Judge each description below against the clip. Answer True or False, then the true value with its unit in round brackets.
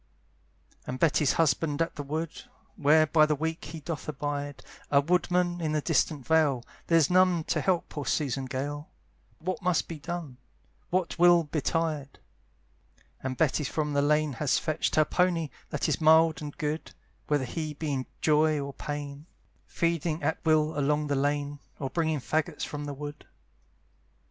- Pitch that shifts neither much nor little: False (2.1 semitones)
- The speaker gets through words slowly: False (165 wpm)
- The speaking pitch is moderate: True (150 Hz)